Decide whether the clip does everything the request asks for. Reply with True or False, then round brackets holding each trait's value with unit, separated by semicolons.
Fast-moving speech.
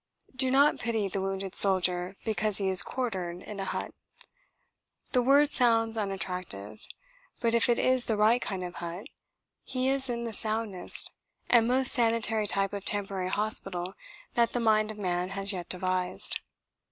False (165 wpm)